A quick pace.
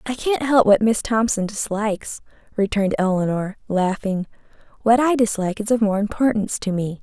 No: average, 160 wpm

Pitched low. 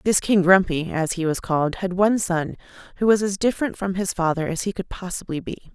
No: medium, 185 Hz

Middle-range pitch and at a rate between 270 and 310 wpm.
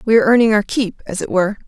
No: high, 215 Hz; fast, 285 wpm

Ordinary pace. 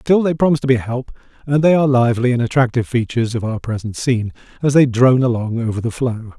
No: fast, 235 wpm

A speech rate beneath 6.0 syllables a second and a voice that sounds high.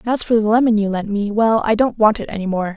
No: 6.5 syllables/s; high, 215 Hz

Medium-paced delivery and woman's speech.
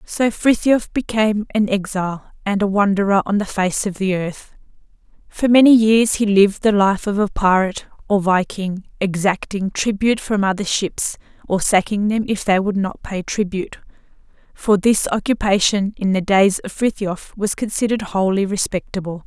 Yes: average, 160 wpm; female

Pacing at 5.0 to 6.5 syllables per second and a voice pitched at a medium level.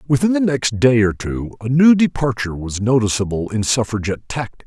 No: 5.7 syllables/s; low, 120 Hz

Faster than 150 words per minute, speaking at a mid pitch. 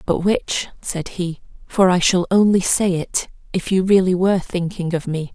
Yes: average, 180 wpm; medium, 180 Hz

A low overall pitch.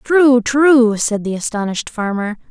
No: high, 240 Hz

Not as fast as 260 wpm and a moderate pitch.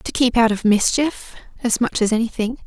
No: average, 200 wpm; high, 235 Hz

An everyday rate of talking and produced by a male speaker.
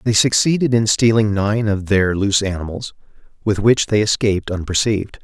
Yes: average, 160 wpm; male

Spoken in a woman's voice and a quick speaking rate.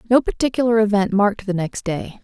No: female; average, 190 wpm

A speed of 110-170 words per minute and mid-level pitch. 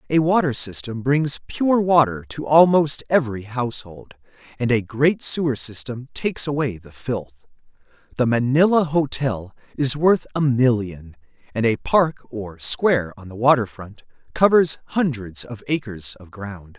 No: average, 145 wpm; low, 125 Hz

